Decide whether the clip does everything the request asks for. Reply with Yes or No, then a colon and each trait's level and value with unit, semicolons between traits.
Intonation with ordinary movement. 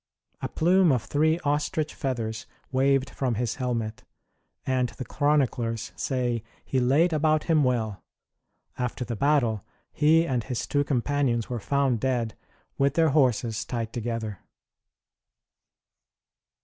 Yes: average, 3.6 semitones